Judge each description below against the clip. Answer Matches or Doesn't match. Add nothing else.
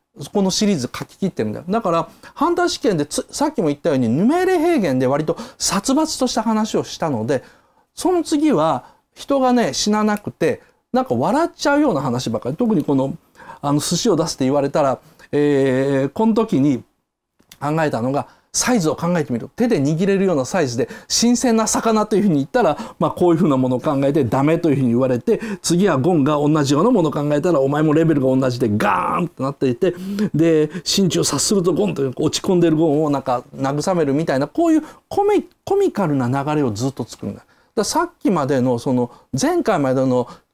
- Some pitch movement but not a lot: Doesn't match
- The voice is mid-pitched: Matches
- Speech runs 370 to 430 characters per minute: Matches